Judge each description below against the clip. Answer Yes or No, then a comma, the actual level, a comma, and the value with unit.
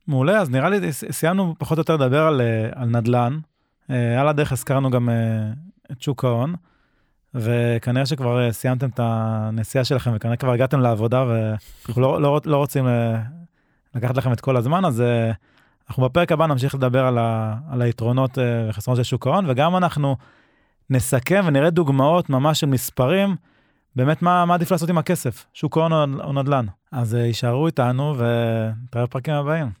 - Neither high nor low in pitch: No, low, 130 Hz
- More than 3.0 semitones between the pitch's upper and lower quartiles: Yes, average, 4.3 semitones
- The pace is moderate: No, fast, 155 wpm